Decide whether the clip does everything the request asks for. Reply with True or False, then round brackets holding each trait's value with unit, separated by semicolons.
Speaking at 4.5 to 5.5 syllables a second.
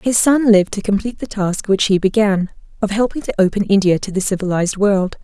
False (6.0 syllables/s)